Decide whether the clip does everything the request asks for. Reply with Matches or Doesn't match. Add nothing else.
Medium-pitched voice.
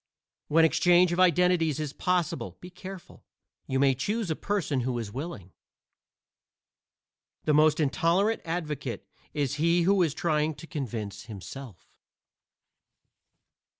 Matches